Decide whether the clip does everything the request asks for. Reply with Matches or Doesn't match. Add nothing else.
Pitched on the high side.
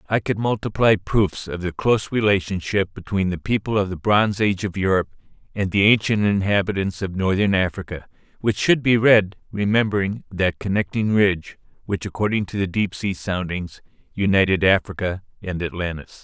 Doesn't match